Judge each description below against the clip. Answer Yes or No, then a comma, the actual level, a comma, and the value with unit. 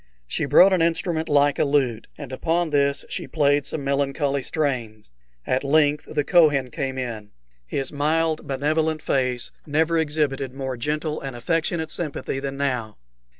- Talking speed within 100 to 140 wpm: No, average, 150 wpm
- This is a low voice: No, medium, 145 Hz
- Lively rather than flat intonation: No, average, 2.8 semitones